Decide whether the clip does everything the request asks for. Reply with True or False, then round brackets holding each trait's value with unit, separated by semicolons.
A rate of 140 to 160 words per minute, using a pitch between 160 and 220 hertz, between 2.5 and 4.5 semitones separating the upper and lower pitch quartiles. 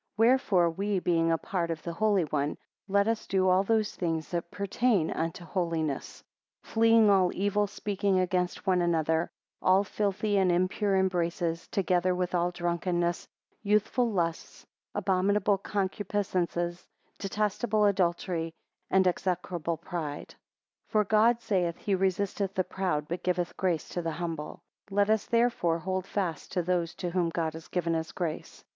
True (150 wpm; 185 Hz; 2.9 semitones)